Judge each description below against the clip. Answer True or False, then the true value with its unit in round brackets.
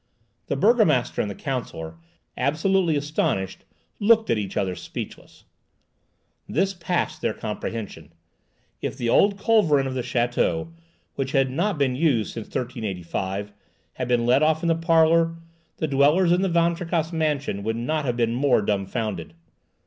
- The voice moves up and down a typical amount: False (6.4 semitones)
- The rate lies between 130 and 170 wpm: True (150 wpm)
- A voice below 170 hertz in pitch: True (140 Hz)